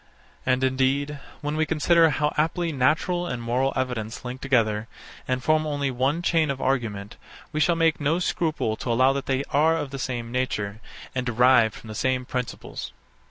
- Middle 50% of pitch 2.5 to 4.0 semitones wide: Yes, average, 3.7 semitones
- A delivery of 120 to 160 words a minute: No, average, 180 wpm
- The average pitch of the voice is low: Yes, low, 130 Hz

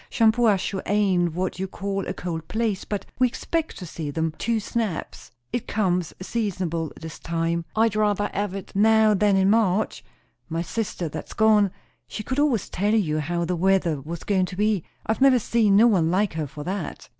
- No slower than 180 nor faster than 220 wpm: Yes, average, 190 wpm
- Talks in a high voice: Yes, high, 195 Hz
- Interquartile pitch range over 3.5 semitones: Yes, average, 4.2 semitones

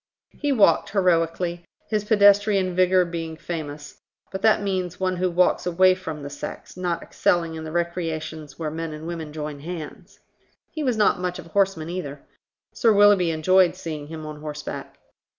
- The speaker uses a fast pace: No, average, 170 wpm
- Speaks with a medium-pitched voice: Yes, medium, 175 Hz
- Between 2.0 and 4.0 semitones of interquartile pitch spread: Yes, average, 2.9 semitones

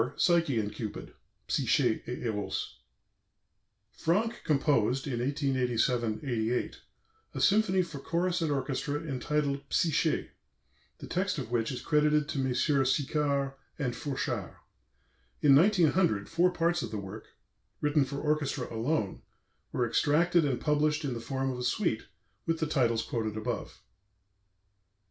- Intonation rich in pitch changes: No, average, 4.5 semitones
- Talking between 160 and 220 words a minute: No, slow, 135 wpm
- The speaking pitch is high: No, medium, 140 Hz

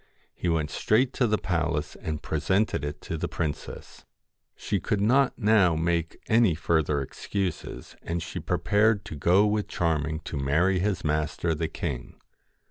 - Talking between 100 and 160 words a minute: Yes, average, 155 wpm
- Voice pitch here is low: Yes, very low, 85 Hz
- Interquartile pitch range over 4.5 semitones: Yes, average, 4.9 semitones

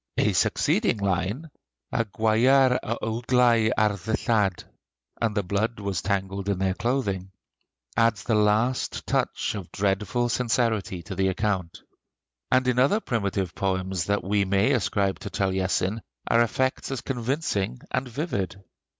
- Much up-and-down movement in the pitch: No, average, 3.8 semitones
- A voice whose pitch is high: No, low, 105 Hz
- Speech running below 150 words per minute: Yes, average, 140 wpm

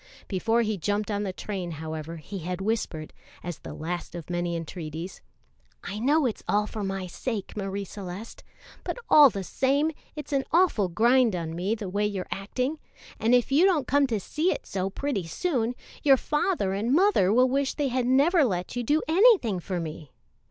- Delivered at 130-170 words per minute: No, average, 190 wpm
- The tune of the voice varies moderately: No, wide, 6.7 semitones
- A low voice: No, high, 210 Hz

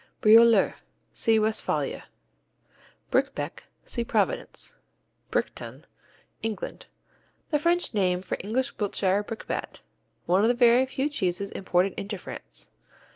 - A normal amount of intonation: Yes, average, 3.6 semitones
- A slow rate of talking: Yes, slow, 110 wpm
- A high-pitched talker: Yes, high, 220 Hz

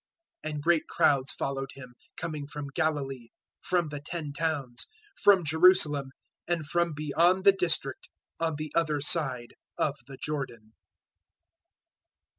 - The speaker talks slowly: Yes, slow, 130 wpm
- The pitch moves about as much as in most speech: Yes, average, 3.3 semitones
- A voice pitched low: No, medium, 150 Hz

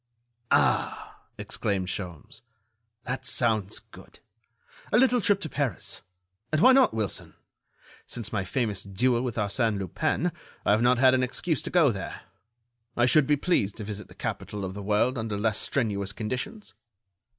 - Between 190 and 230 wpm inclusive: No, average, 160 wpm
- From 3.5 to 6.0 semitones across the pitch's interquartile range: Yes, average, 4.4 semitones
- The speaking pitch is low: Yes, low, 115 Hz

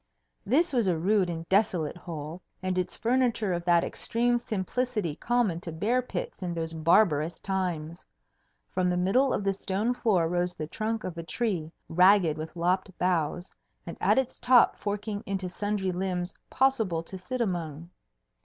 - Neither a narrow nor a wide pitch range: Yes, average, 4.2 semitones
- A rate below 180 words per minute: Yes, average, 165 wpm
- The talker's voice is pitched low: No, medium, 185 Hz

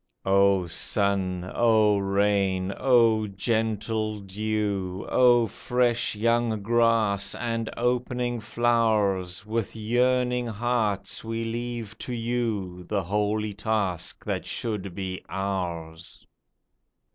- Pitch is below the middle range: Yes, low, 110 Hz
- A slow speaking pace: Yes, slow, 100 wpm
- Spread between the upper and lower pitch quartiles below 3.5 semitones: Yes, average, 3.1 semitones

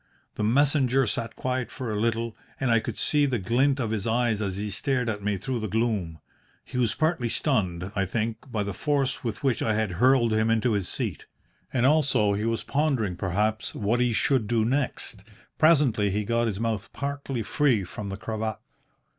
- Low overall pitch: Yes, low, 115 Hz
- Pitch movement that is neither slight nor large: Yes, average, 3.7 semitones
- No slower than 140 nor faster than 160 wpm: No, average, 195 wpm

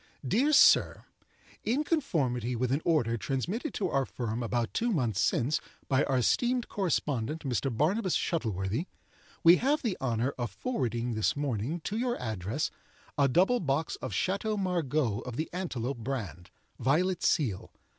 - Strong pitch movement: Yes, wide, 7.7 semitones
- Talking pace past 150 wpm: No, average, 145 wpm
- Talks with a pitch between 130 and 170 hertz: Yes, medium, 140 Hz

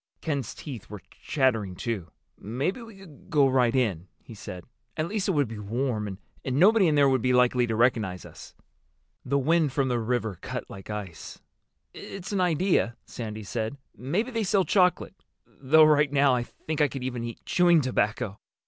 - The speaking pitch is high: No, low, 130 Hz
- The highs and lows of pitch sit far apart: Yes, wide, 5.9 semitones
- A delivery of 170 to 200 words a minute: Yes, average, 185 wpm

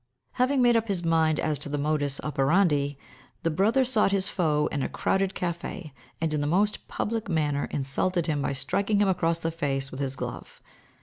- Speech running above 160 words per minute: Yes, average, 195 wpm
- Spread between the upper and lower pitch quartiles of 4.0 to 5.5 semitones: Yes, average, 5.1 semitones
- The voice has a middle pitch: Yes, medium, 165 Hz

